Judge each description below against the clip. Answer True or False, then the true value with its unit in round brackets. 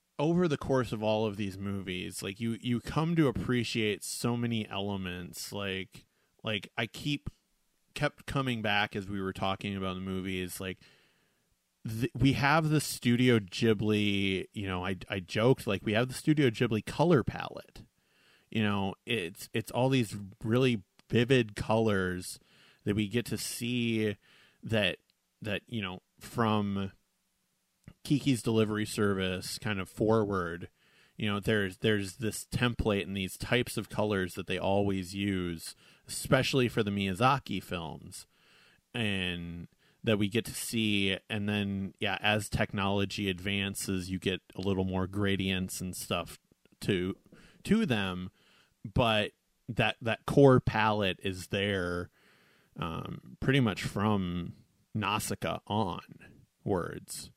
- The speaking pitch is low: True (105 Hz)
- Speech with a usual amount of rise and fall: True (3.8 semitones)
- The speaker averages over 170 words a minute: False (140 wpm)